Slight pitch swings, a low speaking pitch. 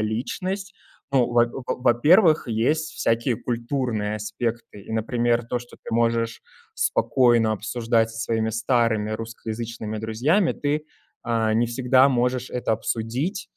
Yes: narrow, 2.1 semitones; low, 115 Hz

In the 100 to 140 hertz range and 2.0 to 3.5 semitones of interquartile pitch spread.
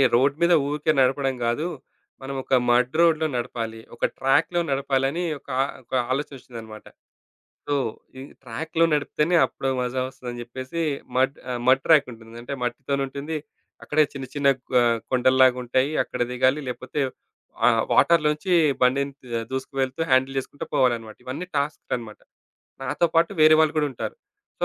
Yes: low, 135 Hz; average, 2.9 semitones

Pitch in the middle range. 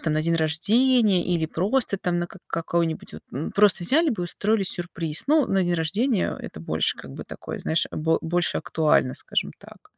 Yes: medium, 175 Hz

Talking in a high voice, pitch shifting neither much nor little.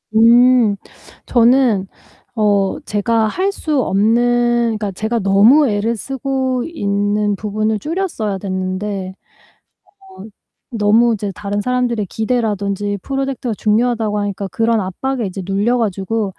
Yes: high, 220 Hz; average, 3.1 semitones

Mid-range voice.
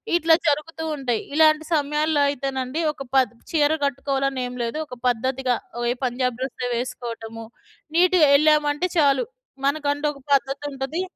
No: very high, 275 Hz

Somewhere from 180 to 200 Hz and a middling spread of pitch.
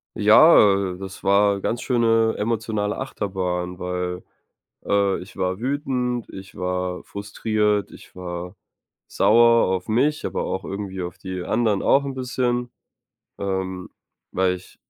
No: low, 100 Hz; average, 4.1 semitones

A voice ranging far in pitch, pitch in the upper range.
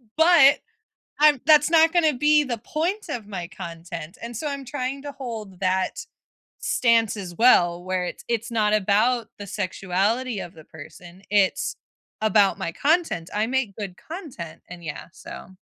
Yes: wide, 7.0 semitones; high, 220 Hz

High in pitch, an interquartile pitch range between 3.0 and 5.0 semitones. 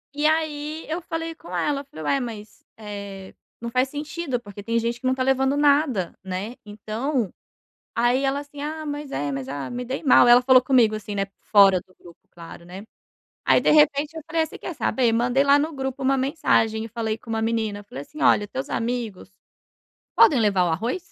No: high, 245 Hz; wide, 5.5 semitones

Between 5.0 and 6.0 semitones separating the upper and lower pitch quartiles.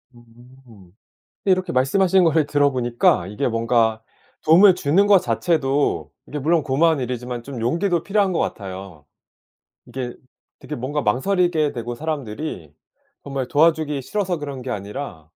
Yes: wide, 5.5 semitones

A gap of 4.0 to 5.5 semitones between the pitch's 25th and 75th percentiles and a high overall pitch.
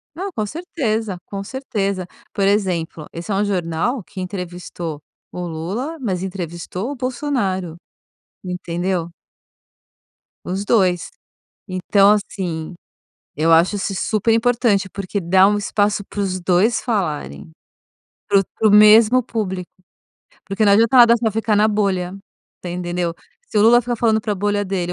No: average, 3.4 semitones; high, 200 Hz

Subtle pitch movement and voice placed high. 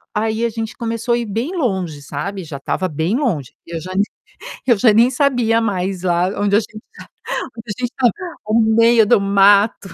No: average, 3.7 semitones; high, 215 Hz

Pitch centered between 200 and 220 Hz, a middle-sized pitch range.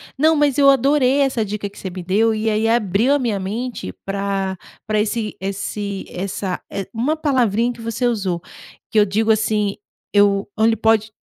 Yes: high, 215 Hz; average, 3.3 semitones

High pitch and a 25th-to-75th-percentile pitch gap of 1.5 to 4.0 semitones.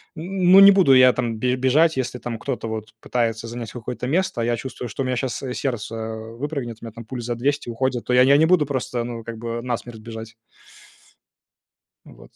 No: low, 120 Hz; narrow, 2.4 semitones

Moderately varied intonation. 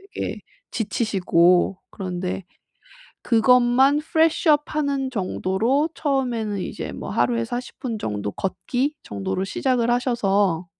No: wide, 6.2 semitones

